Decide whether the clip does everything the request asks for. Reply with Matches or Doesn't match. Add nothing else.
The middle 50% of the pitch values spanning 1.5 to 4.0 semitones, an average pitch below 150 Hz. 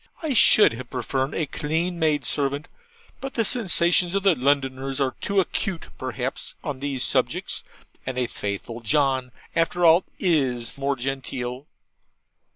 Doesn't match